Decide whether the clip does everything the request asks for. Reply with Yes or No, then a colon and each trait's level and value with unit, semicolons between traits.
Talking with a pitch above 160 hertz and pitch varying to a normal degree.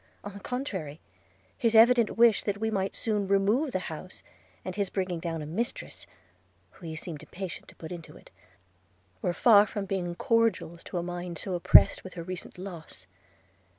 Yes: high, 190 Hz; average, 3.6 semitones